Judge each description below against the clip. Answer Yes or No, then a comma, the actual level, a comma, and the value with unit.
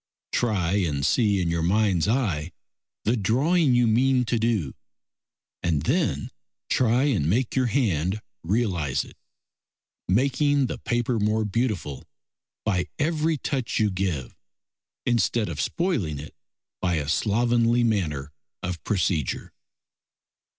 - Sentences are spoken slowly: Yes, slow, 120 wpm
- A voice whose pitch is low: Yes, low, 110 Hz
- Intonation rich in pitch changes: Yes, wide, 6.1 semitones